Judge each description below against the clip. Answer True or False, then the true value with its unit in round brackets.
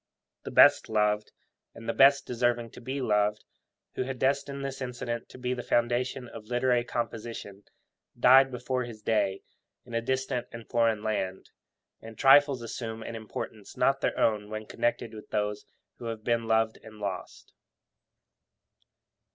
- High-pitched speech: False (115 Hz)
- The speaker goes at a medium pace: True (155 wpm)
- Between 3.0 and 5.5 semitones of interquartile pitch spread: False (2.5 semitones)